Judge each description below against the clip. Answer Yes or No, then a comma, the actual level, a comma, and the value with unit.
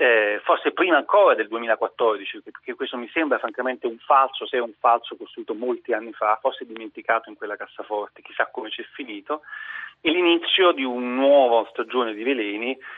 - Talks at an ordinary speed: No, fast, 180 wpm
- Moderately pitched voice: Yes, medium, 175 Hz